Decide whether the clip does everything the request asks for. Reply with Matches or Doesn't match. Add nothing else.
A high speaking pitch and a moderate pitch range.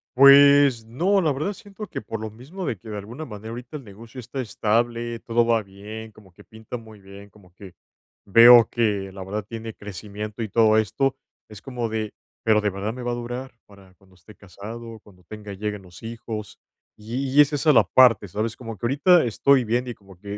Doesn't match